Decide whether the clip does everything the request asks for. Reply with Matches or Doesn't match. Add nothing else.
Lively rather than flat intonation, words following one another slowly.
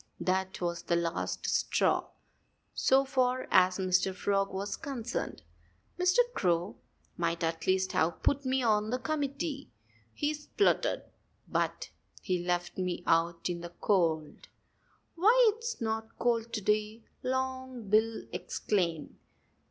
Matches